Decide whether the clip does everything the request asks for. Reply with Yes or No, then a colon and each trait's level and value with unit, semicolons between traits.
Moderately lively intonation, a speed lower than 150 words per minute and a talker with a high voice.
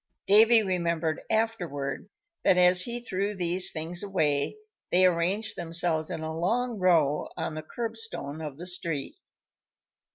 No: average, 4.4 semitones; average, 140 wpm; medium, 180 Hz